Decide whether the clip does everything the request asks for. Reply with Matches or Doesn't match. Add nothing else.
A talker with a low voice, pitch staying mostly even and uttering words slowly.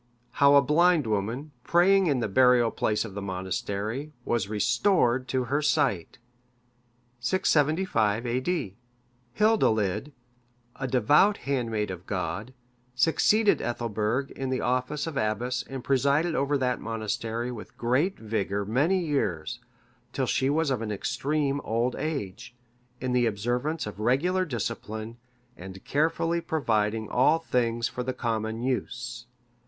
Doesn't match